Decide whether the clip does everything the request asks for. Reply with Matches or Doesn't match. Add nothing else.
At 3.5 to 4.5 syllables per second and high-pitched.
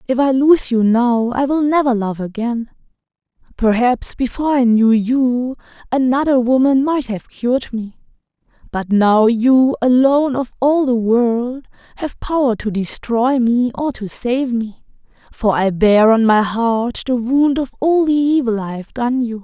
Matches